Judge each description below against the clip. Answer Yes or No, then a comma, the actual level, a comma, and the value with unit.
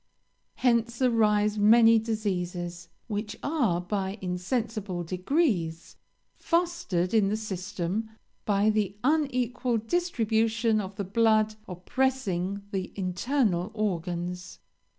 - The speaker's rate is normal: No, slow, 95 wpm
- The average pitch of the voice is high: Yes, high, 210 Hz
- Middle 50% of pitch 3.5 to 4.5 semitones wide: Yes, average, 4.0 semitones